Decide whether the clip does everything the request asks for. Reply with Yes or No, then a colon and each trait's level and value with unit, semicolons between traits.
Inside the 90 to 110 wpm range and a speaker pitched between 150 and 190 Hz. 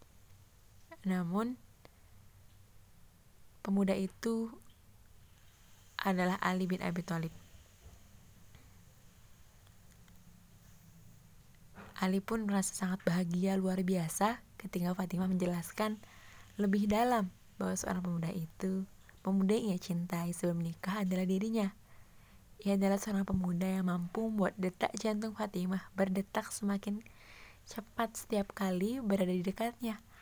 Yes: average, 100 wpm; medium, 185 Hz